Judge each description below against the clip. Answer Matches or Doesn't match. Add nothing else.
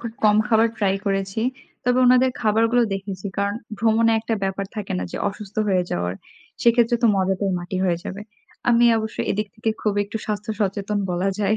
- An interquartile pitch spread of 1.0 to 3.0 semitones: Matches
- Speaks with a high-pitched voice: Matches